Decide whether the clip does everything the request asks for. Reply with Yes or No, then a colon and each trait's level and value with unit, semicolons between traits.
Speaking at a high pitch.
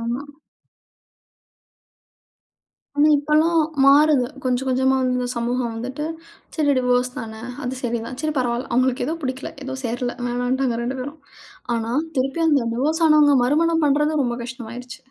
Yes: very high, 255 Hz